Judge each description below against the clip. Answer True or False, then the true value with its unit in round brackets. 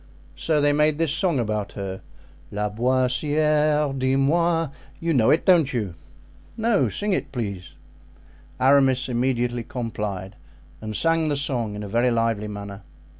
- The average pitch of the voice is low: True (130 Hz)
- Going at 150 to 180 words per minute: False (140 wpm)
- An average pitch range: False (5.8 semitones)